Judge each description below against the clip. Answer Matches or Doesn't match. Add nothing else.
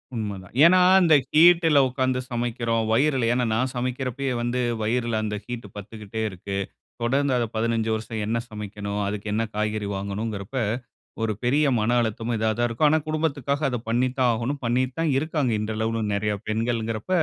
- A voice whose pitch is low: Matches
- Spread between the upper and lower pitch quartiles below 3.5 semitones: Matches